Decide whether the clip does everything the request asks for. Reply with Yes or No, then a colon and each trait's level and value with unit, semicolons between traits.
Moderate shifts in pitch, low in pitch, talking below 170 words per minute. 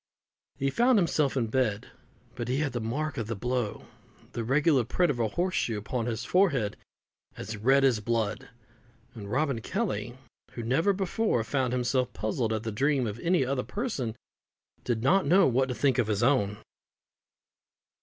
No: average, 4.3 semitones; low, 125 Hz; average, 175 wpm